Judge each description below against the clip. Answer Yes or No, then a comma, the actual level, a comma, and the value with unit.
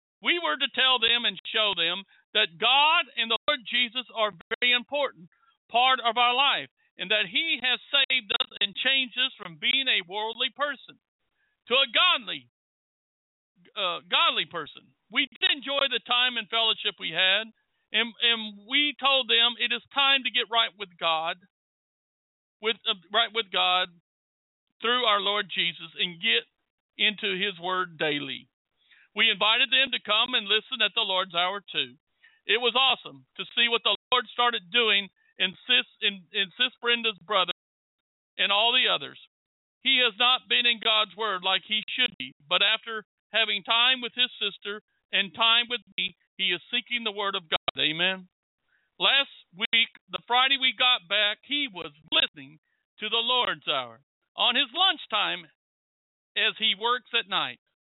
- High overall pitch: Yes, high, 225 Hz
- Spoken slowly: No, average, 170 wpm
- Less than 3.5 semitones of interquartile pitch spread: No, average, 4.3 semitones